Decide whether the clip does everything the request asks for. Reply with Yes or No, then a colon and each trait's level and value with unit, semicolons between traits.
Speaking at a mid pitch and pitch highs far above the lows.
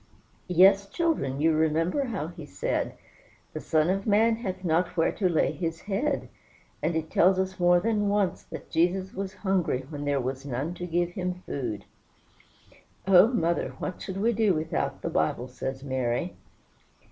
No: medium, 175 Hz; average, 4.0 semitones